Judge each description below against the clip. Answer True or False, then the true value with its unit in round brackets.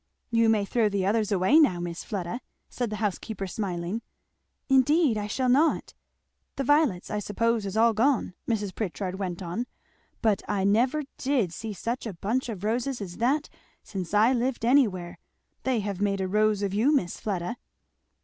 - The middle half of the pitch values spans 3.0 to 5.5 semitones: True (4.0 semitones)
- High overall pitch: True (215 Hz)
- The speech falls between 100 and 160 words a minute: False (180 wpm)